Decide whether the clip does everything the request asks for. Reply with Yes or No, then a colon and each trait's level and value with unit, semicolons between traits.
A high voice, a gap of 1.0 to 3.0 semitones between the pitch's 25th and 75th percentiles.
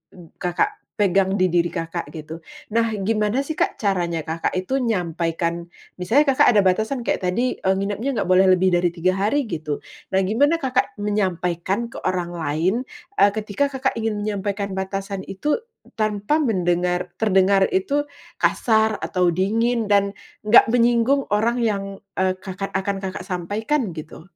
No: high, 195 Hz; average, 3.7 semitones